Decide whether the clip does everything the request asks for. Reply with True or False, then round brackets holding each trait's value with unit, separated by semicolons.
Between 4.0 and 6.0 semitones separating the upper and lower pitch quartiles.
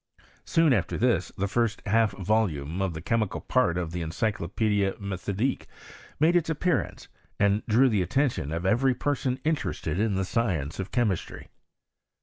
True (5.2 semitones)